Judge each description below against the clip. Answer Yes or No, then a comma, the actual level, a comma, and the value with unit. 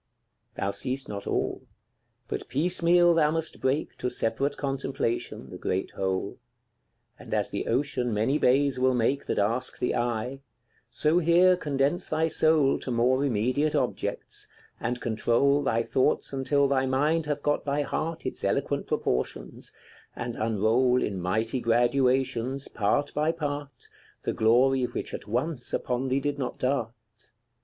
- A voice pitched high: No, low, 130 Hz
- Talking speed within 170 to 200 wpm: No, average, 150 wpm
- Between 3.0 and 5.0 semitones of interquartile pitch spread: Yes, average, 3.6 semitones